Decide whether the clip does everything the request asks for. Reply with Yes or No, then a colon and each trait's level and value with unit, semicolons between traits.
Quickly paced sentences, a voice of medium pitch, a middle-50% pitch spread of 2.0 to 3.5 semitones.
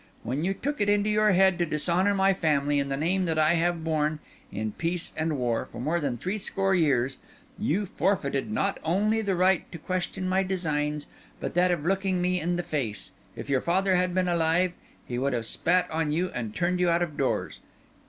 No: fast, 210 wpm; medium, 175 Hz; average, 4.0 semitones